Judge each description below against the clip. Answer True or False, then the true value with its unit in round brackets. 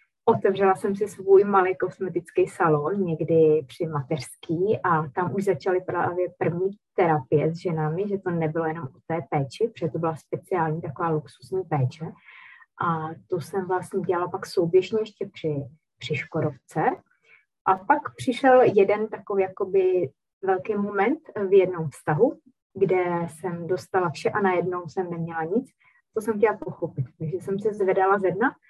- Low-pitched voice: False (180 Hz)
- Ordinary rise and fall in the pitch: True (3.2 semitones)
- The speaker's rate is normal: True (155 wpm)